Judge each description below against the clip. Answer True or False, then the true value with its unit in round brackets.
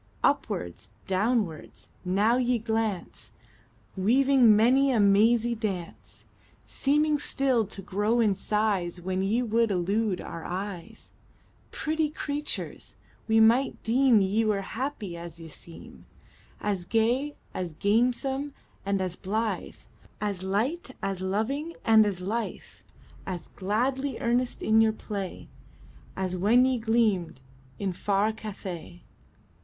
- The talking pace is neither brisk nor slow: False (120 wpm)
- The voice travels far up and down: False (4.1 semitones)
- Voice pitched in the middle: False (215 Hz)